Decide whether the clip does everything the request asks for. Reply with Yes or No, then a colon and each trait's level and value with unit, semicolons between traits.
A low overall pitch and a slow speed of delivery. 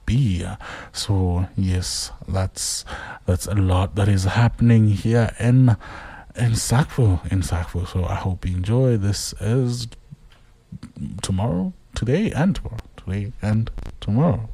Yes: low, 100 Hz; slow, 120 wpm